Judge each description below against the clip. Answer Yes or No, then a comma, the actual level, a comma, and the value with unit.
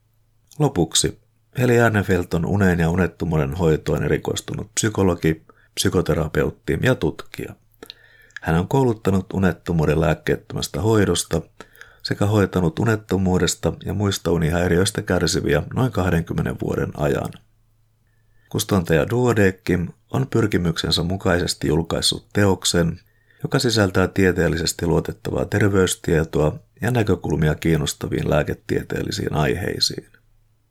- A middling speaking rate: No, slow, 90 wpm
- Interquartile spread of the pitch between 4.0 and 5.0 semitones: Yes, average, 4.6 semitones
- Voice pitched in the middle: No, very low, 95 Hz